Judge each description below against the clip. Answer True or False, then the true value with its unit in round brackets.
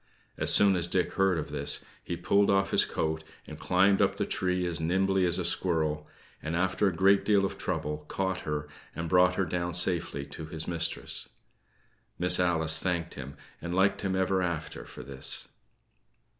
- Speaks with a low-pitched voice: True (90 Hz)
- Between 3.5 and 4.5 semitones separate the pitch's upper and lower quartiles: False (2.9 semitones)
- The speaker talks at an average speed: True (185 wpm)